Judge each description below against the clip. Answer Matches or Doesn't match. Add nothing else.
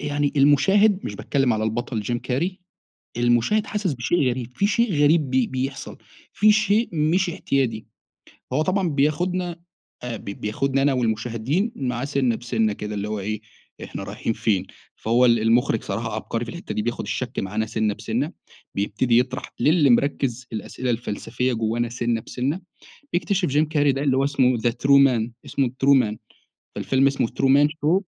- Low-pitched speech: Matches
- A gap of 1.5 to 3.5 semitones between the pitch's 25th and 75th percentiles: Doesn't match